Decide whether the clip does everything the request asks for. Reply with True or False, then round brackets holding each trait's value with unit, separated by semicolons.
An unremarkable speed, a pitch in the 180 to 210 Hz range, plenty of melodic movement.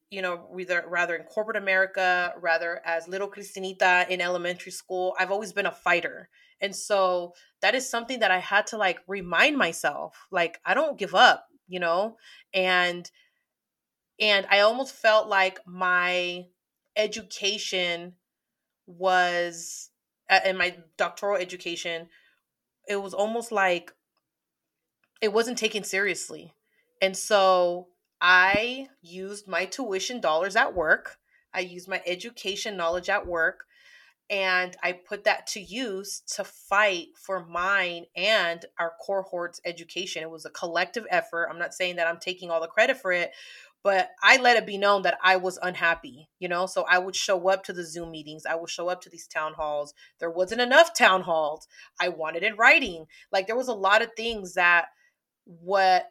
False (165 wpm; 185 Hz; 2.6 semitones)